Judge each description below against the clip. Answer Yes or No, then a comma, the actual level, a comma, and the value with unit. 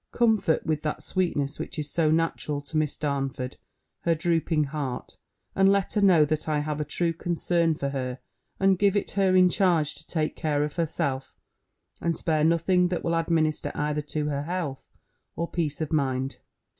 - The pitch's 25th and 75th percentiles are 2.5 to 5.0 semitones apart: Yes, average, 2.8 semitones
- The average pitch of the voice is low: No, medium, 155 Hz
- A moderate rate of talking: Yes, average, 180 wpm